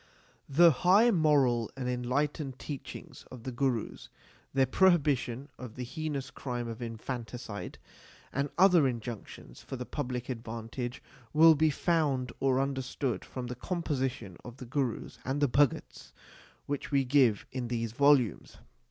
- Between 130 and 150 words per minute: Yes, average, 140 wpm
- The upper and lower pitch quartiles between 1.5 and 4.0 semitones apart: Yes, average, 3.0 semitones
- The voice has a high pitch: No, low, 130 Hz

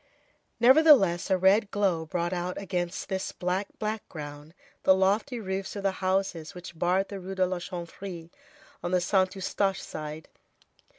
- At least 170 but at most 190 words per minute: No, average, 155 wpm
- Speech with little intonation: Yes, narrow, 2.1 semitones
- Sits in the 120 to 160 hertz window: No, medium, 185 Hz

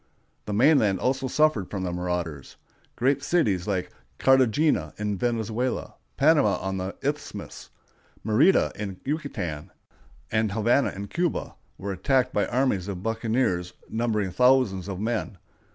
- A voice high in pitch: No, low, 110 Hz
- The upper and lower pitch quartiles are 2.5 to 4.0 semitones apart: No, wide, 5.5 semitones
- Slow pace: Yes, slow, 130 wpm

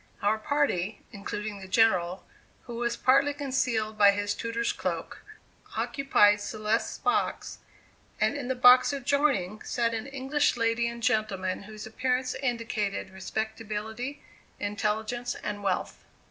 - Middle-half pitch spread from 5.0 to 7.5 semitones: No, average, 3.5 semitones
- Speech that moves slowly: Yes, slow, 125 wpm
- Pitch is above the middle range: Yes, high, 225 Hz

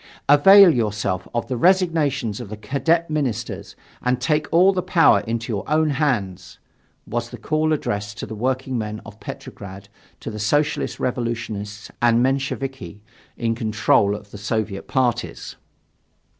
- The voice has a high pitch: No, low, 120 Hz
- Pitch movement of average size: No, wide, 5.7 semitones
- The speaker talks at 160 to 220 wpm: No, average, 145 wpm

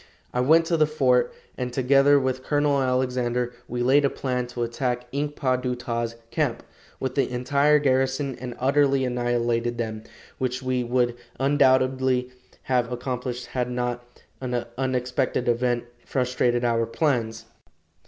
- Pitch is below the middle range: Yes, low, 125 Hz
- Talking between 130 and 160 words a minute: Yes, average, 145 wpm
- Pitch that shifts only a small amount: Yes, narrow, 1.5 semitones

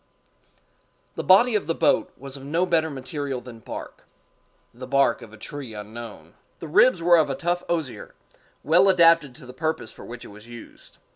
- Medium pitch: Yes, medium, 145 Hz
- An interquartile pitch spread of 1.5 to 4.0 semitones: No, wide, 5.4 semitones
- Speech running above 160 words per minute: Yes, average, 185 wpm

